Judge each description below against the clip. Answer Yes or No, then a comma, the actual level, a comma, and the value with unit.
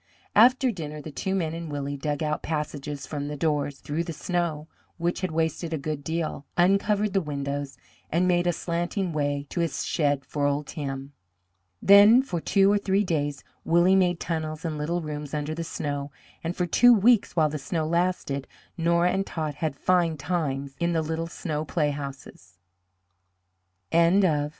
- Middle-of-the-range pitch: Yes, medium, 160 Hz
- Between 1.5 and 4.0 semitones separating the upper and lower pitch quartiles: Yes, average, 3.2 semitones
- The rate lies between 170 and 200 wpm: Yes, average, 175 wpm